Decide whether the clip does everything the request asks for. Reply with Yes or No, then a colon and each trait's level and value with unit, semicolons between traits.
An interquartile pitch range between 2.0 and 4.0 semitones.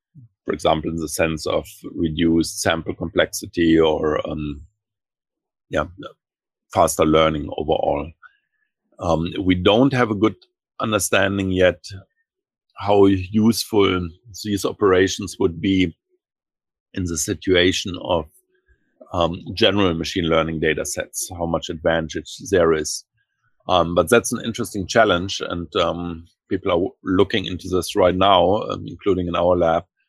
No: average, 4.6 semitones